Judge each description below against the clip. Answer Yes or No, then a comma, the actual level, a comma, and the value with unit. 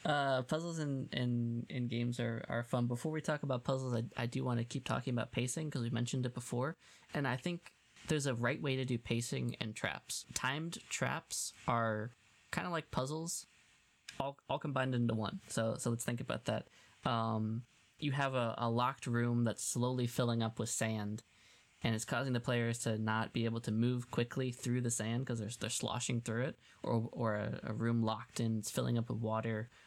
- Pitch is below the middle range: Yes, low, 120 Hz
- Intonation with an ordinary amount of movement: No, narrow, 2.3 semitones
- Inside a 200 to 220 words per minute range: Yes, fast, 205 wpm